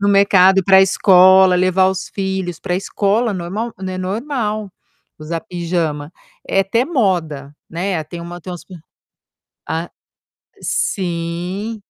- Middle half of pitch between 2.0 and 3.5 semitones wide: Yes, narrow, 2.5 semitones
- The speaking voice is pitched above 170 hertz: Yes, medium, 185 Hz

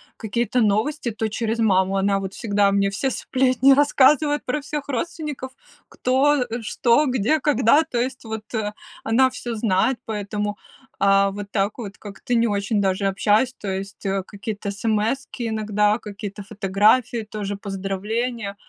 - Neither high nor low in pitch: No, high, 220 Hz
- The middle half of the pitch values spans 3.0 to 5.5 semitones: Yes, average, 4.0 semitones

